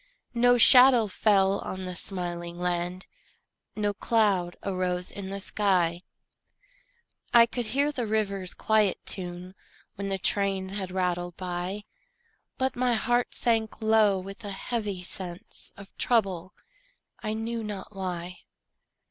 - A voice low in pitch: No, high, 195 Hz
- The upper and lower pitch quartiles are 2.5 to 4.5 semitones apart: Yes, average, 3.2 semitones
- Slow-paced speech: Yes, slow, 130 wpm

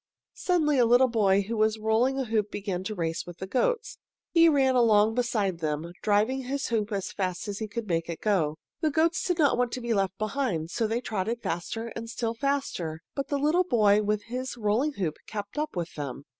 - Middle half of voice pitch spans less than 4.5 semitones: No, average, 4.9 semitones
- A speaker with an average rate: No, fast, 215 wpm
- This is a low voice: No, high, 220 Hz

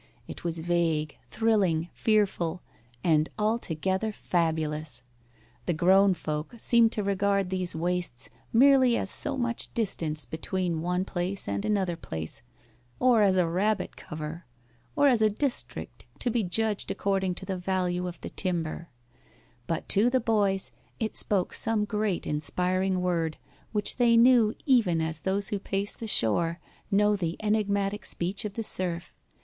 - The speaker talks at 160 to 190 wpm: No, average, 150 wpm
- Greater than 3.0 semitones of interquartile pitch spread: Yes, average, 4.0 semitones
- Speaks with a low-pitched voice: No, high, 190 Hz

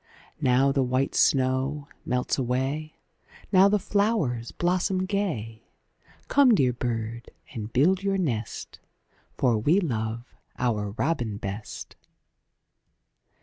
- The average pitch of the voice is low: Yes, low, 130 Hz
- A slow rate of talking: Yes, slow, 105 wpm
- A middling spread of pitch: No, wide, 7.4 semitones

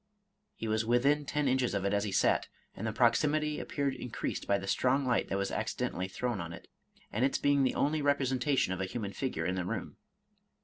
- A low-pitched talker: Yes, low, 125 Hz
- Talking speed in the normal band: No, fast, 220 wpm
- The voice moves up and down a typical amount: No, wide, 5.9 semitones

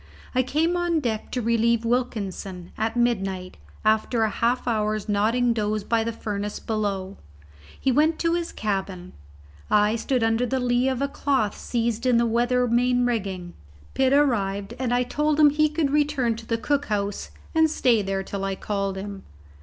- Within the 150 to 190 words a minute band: Yes, average, 175 wpm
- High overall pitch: Yes, high, 230 Hz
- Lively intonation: No, average, 3.8 semitones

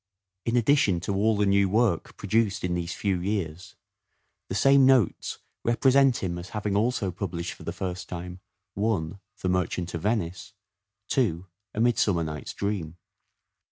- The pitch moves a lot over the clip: No, average, 4.1 semitones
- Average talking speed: Yes, average, 160 wpm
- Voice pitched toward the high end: No, low, 100 Hz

